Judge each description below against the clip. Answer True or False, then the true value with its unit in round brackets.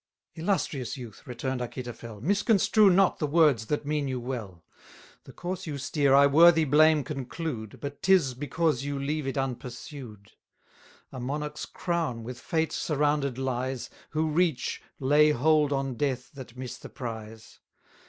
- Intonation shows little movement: False (3.6 semitones)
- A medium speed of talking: True (145 wpm)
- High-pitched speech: False (140 Hz)